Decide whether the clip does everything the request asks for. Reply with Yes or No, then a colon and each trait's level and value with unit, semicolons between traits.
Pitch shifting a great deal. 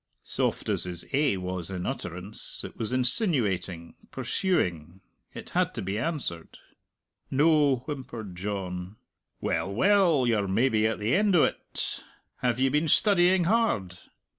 Yes: wide, 8.4 semitones